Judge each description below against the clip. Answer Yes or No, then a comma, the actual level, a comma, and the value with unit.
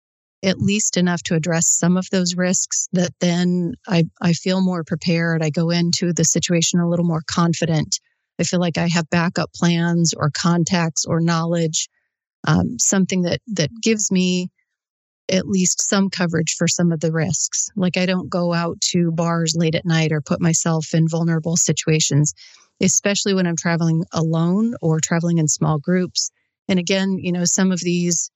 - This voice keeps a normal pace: Yes, average, 180 wpm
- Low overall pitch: No, medium, 170 Hz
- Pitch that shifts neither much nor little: No, narrow, 1.7 semitones